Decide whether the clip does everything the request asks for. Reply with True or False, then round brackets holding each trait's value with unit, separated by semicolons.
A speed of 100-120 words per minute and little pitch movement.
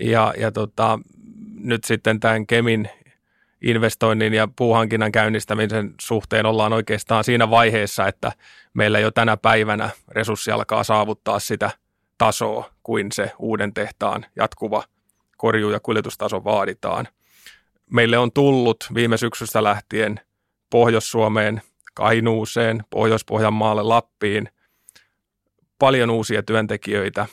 True (105 wpm; 1.1 semitones)